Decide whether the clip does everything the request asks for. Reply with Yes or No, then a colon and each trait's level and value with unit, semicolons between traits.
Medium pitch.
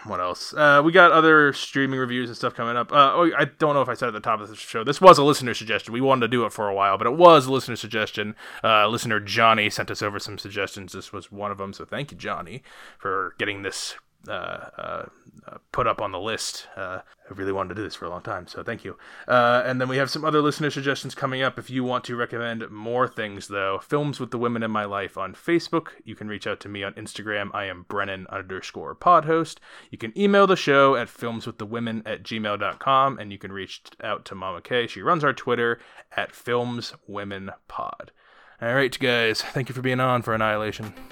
No: low, 115 Hz